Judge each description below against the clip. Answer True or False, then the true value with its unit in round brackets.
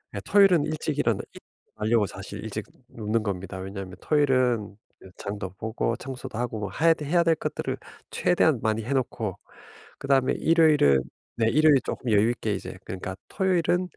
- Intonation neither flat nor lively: False (6.7 semitones)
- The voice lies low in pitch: True (120 Hz)